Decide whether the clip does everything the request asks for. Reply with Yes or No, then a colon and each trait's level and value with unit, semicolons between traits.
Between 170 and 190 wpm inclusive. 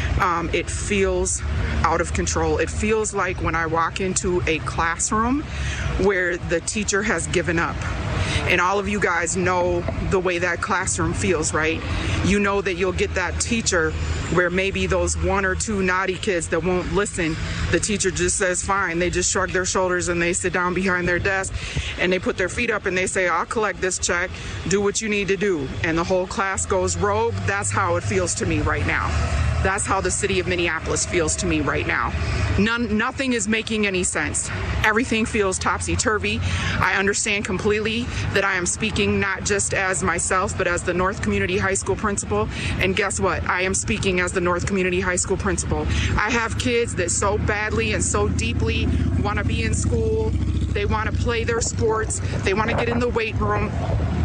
No: average, 200 wpm